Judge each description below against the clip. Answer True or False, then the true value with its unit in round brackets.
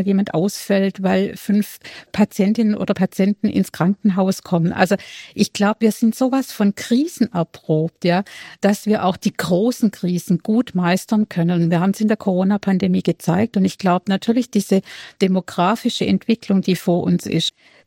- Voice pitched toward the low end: False (195 Hz)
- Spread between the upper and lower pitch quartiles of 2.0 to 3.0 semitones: True (2.7 semitones)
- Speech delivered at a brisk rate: False (160 wpm)